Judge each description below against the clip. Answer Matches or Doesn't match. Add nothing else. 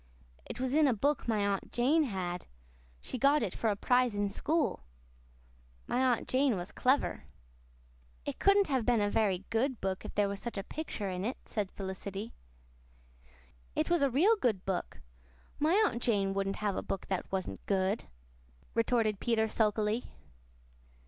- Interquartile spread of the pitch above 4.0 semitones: Matches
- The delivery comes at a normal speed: Matches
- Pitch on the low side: Doesn't match